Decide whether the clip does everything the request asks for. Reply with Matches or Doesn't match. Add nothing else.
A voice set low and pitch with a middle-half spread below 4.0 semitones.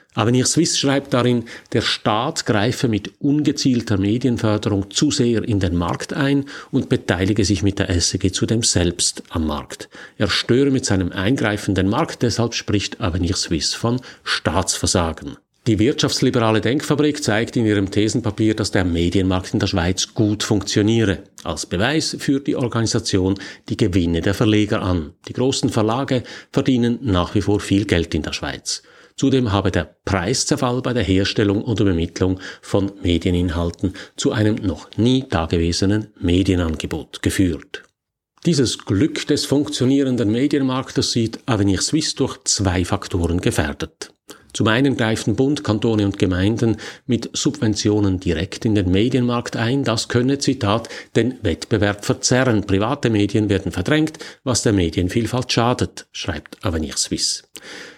Doesn't match